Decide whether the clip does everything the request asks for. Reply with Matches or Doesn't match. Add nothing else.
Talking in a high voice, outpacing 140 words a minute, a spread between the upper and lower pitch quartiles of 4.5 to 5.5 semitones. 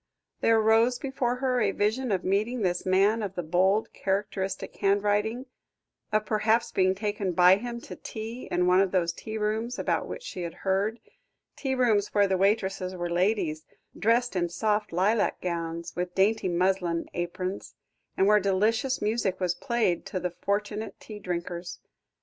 Doesn't match